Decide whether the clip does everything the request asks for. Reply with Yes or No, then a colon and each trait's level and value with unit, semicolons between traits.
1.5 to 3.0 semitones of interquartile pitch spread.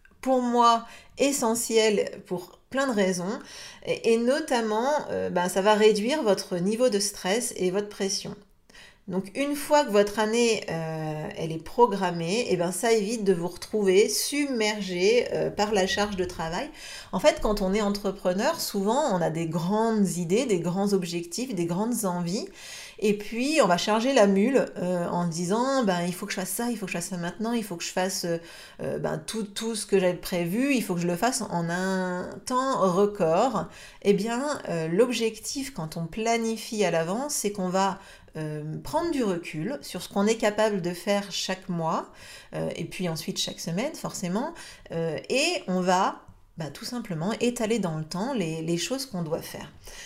No: average, 4.3 semitones